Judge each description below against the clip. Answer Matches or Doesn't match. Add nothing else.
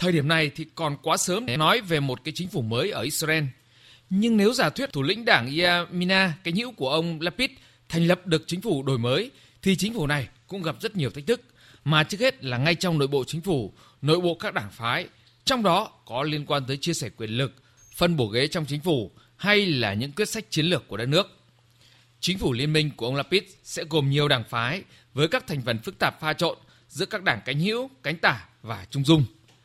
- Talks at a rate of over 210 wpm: Matches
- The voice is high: Doesn't match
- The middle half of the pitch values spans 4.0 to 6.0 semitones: Matches